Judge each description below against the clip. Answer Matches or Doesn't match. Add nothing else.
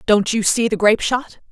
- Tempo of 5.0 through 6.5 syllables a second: Matches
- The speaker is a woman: Matches